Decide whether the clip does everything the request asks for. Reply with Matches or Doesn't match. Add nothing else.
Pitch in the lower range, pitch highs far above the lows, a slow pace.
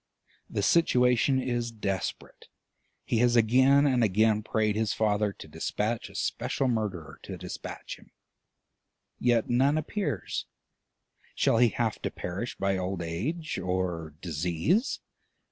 Doesn't match